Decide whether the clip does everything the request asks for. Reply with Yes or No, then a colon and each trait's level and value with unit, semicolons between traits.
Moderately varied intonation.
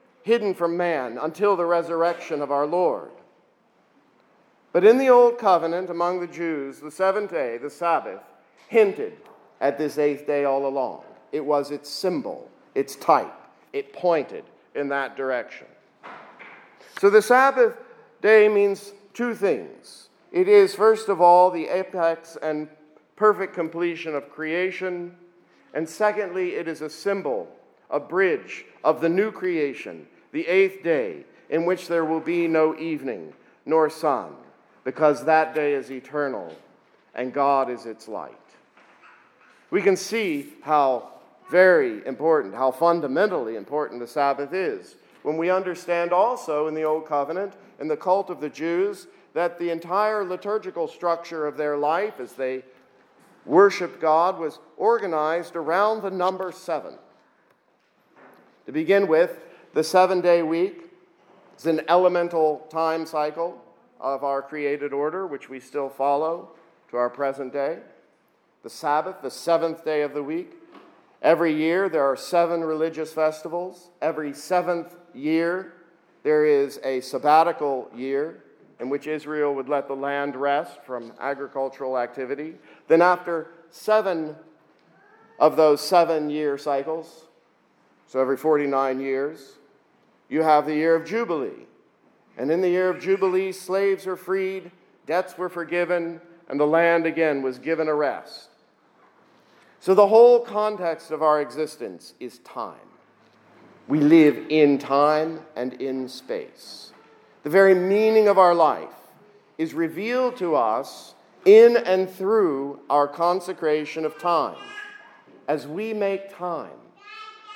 Yes: average, 4.4 semitones